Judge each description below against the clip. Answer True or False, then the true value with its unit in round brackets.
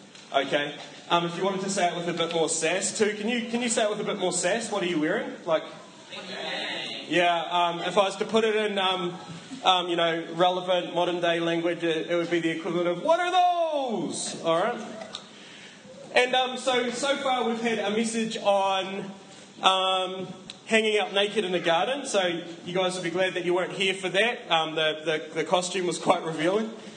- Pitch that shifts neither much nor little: True (3.7 semitones)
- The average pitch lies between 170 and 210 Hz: True (185 Hz)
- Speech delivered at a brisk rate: True (215 wpm)